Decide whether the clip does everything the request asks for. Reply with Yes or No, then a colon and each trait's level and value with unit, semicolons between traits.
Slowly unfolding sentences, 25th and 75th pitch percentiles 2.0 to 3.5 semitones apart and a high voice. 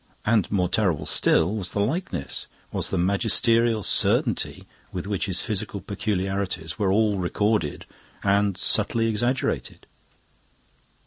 No: slow, 120 wpm; average, 2.8 semitones; low, 100 Hz